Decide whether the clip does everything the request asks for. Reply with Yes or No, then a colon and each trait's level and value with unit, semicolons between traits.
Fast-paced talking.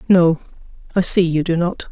No: average, 190 wpm